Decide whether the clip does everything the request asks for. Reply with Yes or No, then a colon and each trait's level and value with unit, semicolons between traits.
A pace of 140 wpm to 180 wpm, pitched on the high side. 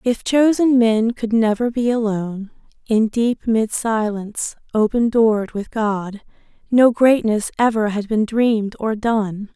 Yes: average, 145 wpm; high, 225 Hz